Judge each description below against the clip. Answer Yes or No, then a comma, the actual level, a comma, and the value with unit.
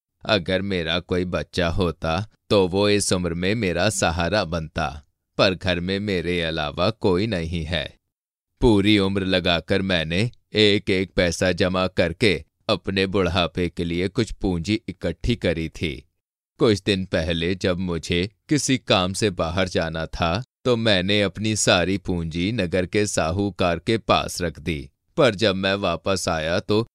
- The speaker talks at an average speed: Yes, average, 150 wpm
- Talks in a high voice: No, very low, 95 Hz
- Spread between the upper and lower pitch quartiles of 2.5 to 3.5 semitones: Yes, average, 3.0 semitones